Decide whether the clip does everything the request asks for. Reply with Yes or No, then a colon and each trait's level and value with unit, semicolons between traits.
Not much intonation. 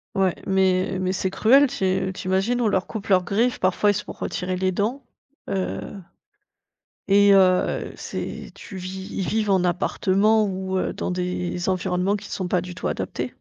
Yes: narrow, 1.7 semitones